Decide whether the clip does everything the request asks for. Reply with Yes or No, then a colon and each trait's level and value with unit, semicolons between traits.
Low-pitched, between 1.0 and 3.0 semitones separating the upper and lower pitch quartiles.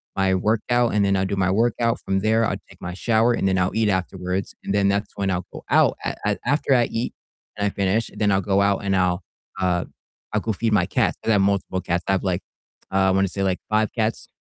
Yes: low, 100 Hz; narrow, 2.4 semitones